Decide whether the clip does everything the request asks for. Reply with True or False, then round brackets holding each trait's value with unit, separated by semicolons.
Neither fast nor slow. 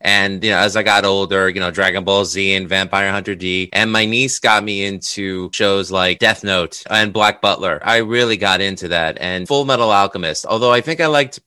False (225 wpm)